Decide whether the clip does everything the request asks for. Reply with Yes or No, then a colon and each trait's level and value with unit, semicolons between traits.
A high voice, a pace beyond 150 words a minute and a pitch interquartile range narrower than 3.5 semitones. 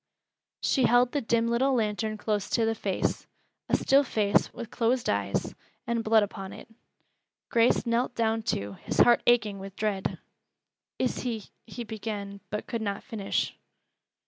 Yes: high, 225 Hz; average, 160 wpm; narrow, 2.6 semitones